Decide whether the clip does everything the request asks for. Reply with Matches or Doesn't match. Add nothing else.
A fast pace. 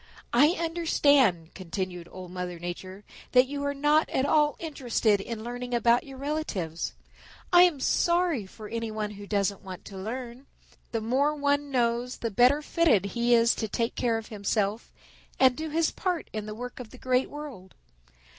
Doesn't match